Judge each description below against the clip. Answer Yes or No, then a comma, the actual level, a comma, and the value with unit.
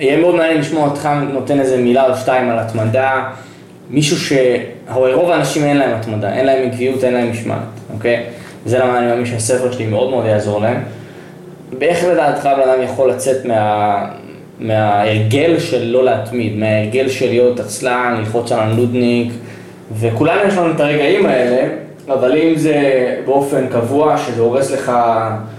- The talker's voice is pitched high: No, low, 125 Hz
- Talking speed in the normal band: No, fast, 155 wpm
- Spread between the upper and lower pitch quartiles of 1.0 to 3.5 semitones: Yes, average, 3.0 semitones